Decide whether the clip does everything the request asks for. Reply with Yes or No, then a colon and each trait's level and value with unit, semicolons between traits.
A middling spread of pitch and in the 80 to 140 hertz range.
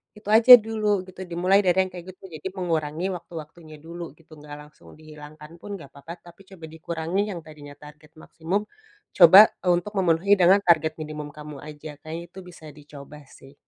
No: average, 3.6 semitones; medium, 165 Hz